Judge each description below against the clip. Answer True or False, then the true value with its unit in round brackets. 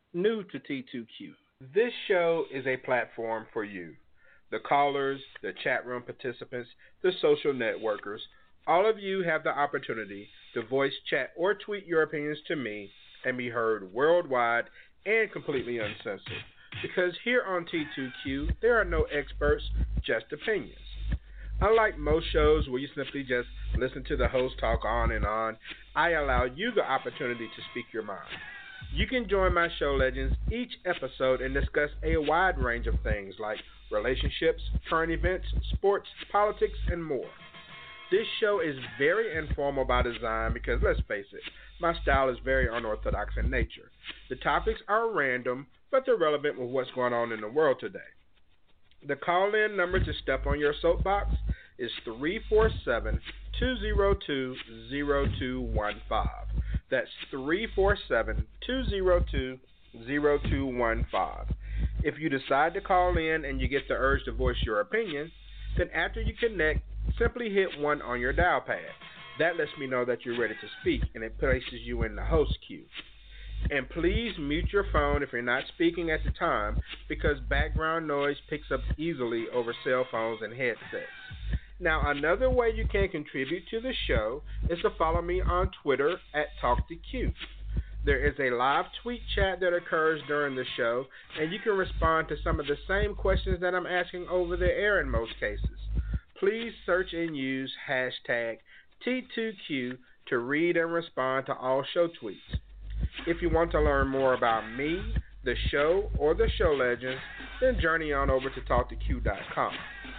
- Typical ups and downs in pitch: False (6.6 semitones)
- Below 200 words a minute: True (160 wpm)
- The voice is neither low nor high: True (150 Hz)